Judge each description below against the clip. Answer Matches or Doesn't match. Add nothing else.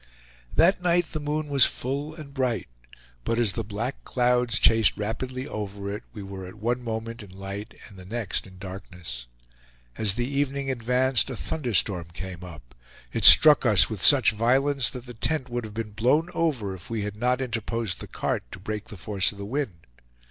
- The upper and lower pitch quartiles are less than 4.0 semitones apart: Doesn't match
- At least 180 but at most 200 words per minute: Matches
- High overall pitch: Doesn't match